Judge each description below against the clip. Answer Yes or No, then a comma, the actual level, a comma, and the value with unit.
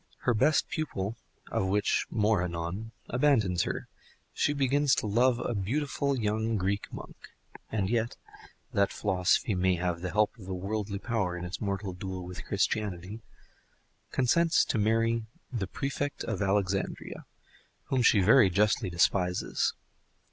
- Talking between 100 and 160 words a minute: Yes, average, 140 wpm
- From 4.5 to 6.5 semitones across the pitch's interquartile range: No, average, 3.8 semitones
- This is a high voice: No, low, 105 Hz